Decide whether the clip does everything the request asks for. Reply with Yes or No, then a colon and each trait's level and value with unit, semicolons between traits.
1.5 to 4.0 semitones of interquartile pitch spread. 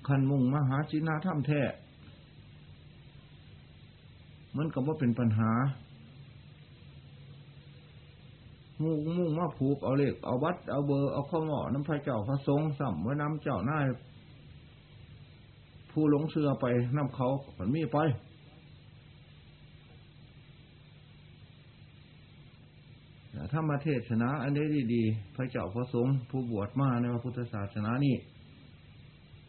Yes: average, 2.7 semitones